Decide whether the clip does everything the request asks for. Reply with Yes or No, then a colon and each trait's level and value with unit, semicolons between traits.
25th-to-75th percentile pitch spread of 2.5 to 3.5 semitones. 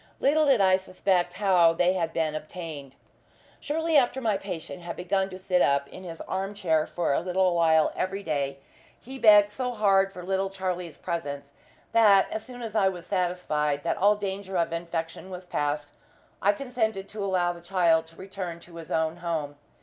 Yes: average, 3.1 semitones